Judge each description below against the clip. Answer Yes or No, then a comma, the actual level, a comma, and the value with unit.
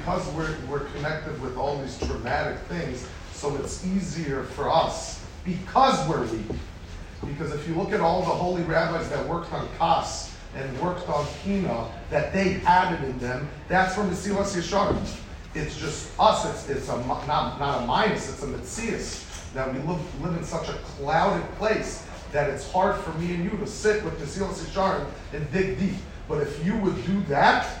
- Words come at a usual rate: Yes, average, 190 wpm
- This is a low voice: No, medium, 175 Hz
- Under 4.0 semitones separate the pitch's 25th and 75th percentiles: No, average, 4.6 semitones